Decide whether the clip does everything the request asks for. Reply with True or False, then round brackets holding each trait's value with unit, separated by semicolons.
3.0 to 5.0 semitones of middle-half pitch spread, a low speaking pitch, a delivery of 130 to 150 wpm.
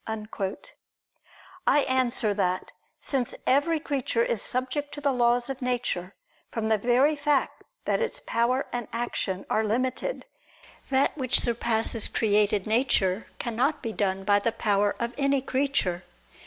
False (3.9 semitones; 240 Hz; 140 wpm)